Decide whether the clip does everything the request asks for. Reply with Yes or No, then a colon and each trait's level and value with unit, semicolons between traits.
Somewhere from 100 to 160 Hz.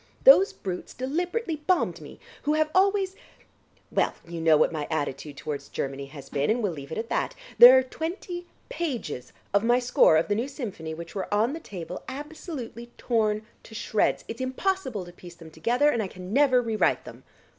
No: high, 230 Hz